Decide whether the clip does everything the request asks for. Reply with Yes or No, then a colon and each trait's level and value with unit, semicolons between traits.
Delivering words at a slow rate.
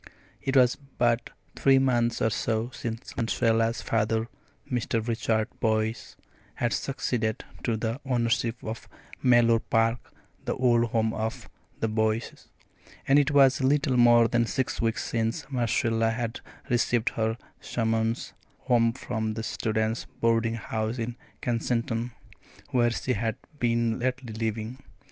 Yes: slow, 130 wpm